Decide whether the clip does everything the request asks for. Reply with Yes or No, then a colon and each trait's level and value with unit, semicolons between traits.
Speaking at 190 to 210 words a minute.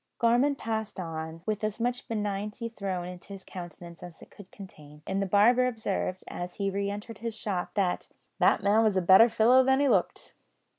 Yes: average, 195 wpm